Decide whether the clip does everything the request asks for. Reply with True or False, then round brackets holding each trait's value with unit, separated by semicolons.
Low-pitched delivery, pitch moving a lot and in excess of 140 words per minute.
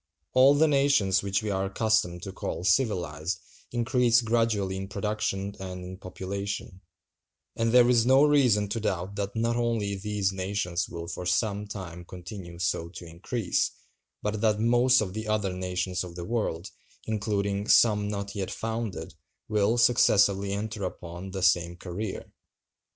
False (100 Hz; 3.3 semitones; 155 wpm)